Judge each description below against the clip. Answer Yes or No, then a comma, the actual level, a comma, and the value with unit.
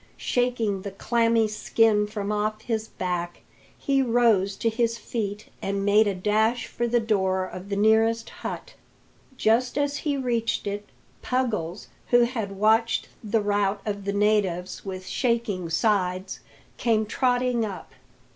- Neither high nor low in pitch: No, high, 215 Hz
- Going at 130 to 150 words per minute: Yes, average, 145 wpm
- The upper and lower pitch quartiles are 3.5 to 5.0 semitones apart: No, average, 2.7 semitones